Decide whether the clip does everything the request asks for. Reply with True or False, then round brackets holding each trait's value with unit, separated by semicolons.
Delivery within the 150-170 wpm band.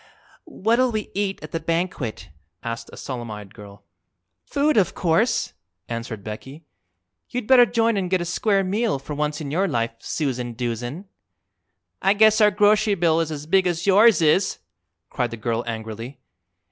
True (165 wpm)